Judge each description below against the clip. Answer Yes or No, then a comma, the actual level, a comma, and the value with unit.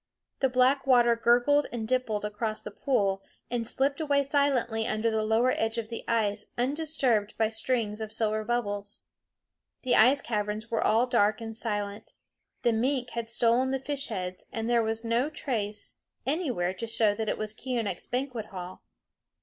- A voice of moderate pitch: No, high, 230 Hz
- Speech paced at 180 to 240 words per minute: No, average, 165 wpm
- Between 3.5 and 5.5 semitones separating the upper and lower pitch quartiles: No, average, 2.9 semitones